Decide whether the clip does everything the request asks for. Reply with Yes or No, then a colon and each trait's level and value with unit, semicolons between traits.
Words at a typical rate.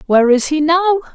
No: fast, 210 wpm